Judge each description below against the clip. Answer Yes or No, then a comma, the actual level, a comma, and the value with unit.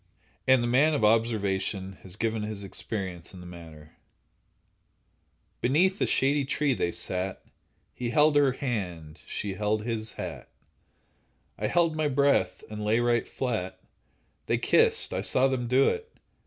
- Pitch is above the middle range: No, low, 115 Hz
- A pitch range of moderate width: No, wide, 5.8 semitones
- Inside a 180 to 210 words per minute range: No, average, 145 wpm